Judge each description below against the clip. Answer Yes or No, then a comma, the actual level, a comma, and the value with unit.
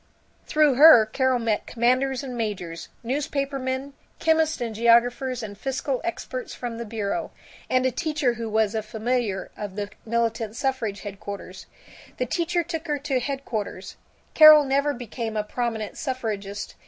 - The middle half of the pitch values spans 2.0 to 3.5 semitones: No, average, 4.1 semitones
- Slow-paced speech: No, average, 145 wpm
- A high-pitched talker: Yes, high, 245 Hz